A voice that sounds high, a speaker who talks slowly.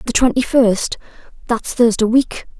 Yes: high, 230 Hz; slow, 115 wpm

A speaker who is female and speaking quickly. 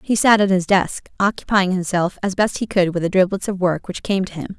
Yes: female; fast, 260 wpm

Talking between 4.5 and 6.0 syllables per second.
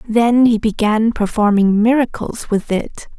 No: 4.0 syllables/s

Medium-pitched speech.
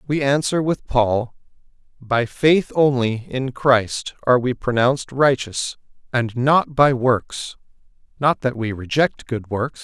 No: low, 130 Hz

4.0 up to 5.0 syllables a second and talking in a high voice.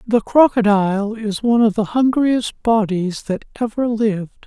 Yes: 4.7 syllables/s; high, 220 Hz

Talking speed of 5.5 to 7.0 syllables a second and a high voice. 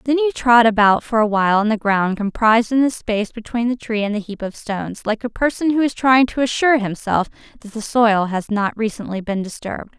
Yes: 5.7 syllables/s; high, 225 Hz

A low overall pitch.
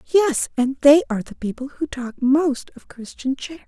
No: very high, 275 Hz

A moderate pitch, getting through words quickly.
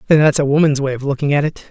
Yes: medium, 145 Hz; fast, 280 wpm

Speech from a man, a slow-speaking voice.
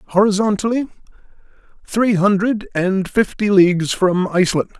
Yes: male; slow, 100 wpm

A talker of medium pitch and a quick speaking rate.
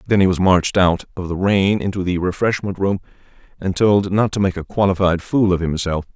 No: very low, 95 Hz; fast, 215 wpm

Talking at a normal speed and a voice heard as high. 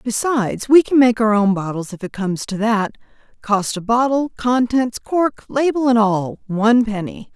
Yes: average, 180 wpm; high, 225 Hz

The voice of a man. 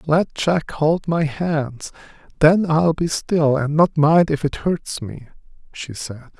Yes: male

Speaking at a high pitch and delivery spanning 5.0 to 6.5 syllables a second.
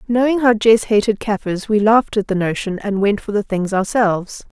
Yes: high, 210 Hz; 5.3 syllables/s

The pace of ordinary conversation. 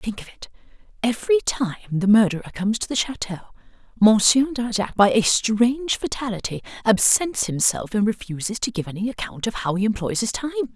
Yes: average, 165 wpm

